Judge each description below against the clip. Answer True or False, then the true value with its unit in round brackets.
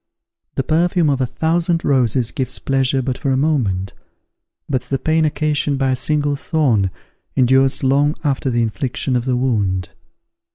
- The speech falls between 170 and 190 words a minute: False (160 wpm)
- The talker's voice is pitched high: False (135 Hz)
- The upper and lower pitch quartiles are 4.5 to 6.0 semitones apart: False (3.0 semitones)